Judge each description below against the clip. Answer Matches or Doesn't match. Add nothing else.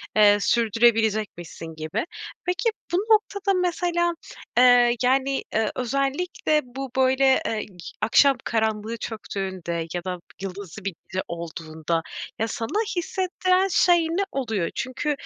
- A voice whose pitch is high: Matches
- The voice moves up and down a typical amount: Doesn't match